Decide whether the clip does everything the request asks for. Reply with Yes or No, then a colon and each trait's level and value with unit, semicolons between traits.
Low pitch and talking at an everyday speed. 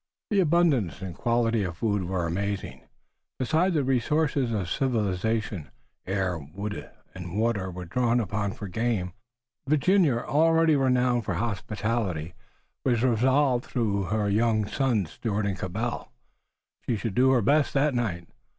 Yes: low, 115 Hz; average, 145 wpm